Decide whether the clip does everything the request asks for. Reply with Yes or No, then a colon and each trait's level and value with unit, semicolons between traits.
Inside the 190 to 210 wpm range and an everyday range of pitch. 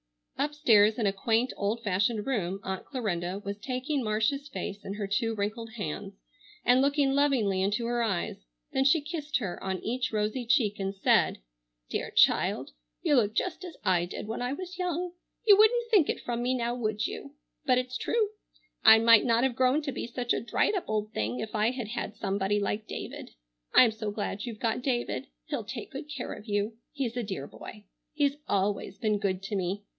Yes: average, 200 wpm; average, 4.5 semitones